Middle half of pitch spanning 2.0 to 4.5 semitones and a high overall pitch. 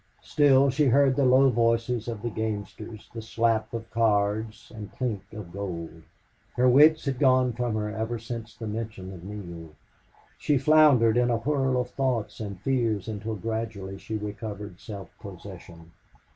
No: average, 3.3 semitones; low, 115 Hz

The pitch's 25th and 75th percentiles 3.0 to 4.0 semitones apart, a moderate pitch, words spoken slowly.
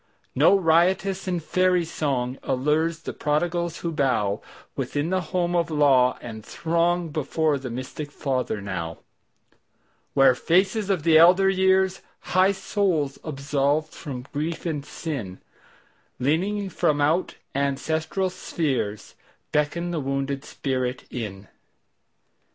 No: average, 4.4 semitones; medium, 155 Hz; slow, 100 wpm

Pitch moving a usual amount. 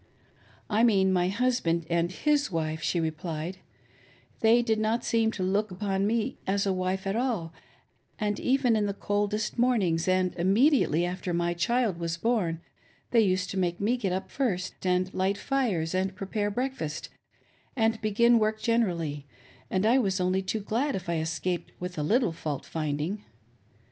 Yes: average, 4.4 semitones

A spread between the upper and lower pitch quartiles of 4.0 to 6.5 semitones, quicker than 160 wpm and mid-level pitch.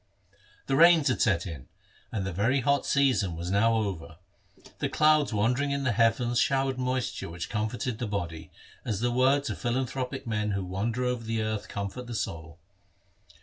No: average, 4.4 semitones; average, 175 wpm; low, 115 Hz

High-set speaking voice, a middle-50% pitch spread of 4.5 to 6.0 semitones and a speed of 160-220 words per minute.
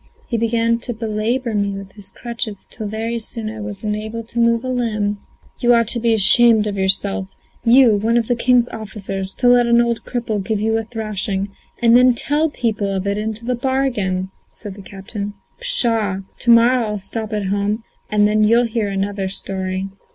No: high, 220 Hz; average, 2.7 semitones; average, 195 wpm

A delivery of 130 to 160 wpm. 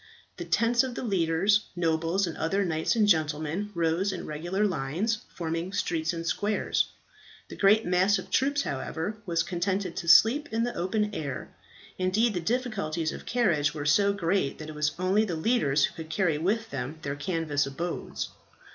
No: average, 175 wpm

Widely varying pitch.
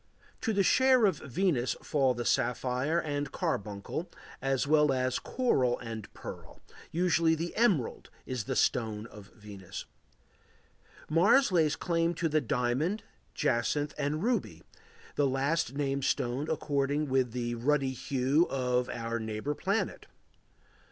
No: average, 4.9 semitones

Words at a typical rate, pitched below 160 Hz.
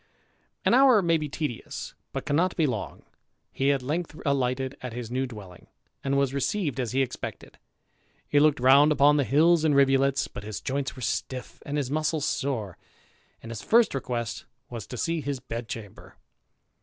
Yes: average, 180 wpm; low, 135 Hz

